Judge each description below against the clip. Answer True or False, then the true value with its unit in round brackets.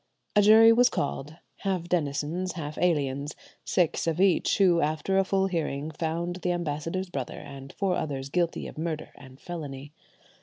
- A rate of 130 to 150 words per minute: False (160 wpm)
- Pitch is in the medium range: True (165 Hz)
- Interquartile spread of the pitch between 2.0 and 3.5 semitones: False (3.9 semitones)